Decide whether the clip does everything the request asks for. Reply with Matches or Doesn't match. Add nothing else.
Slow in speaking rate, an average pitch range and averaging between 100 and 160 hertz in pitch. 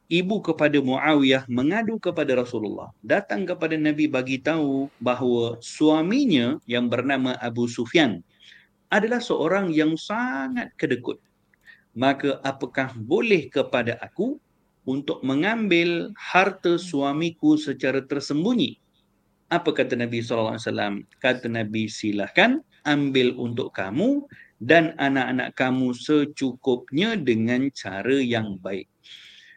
Matches